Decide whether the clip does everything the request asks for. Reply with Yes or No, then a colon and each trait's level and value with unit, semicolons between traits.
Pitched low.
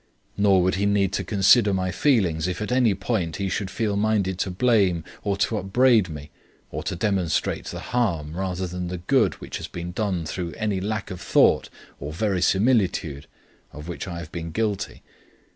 Yes: very low, 95 Hz